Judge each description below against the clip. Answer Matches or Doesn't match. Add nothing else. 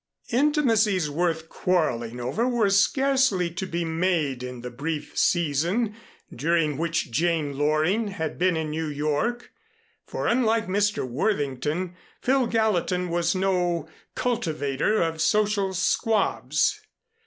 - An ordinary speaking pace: Doesn't match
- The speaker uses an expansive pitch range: Matches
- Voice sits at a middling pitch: Matches